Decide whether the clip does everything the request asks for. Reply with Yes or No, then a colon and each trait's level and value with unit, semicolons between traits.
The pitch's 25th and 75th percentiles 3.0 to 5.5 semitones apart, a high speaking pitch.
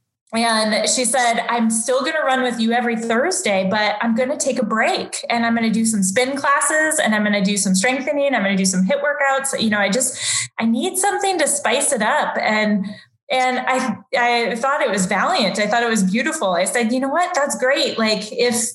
Yes: average, 4.2 semitones; high, 235 Hz